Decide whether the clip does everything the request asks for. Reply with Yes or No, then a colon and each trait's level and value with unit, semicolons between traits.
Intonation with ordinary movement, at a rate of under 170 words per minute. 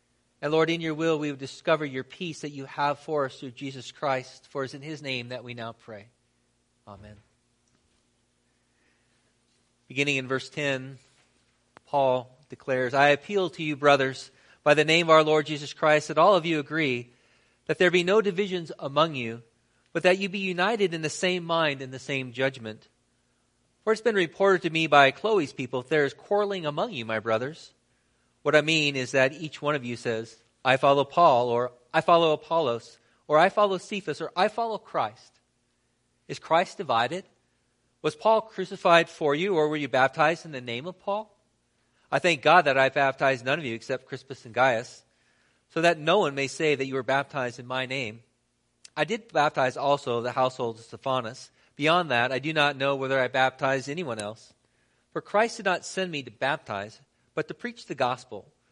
No: average, 4.2 semitones; average, 195 wpm